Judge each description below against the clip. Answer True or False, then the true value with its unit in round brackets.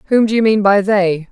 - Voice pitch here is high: True (205 Hz)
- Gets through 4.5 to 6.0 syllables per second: True (5.5 syllables/s)